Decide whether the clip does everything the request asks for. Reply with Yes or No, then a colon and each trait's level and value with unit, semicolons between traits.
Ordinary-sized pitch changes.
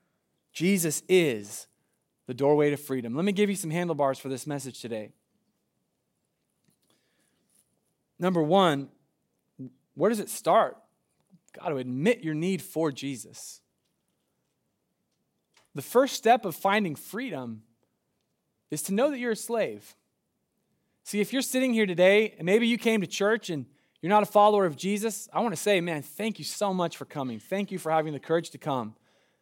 No: wide, 6.4 semitones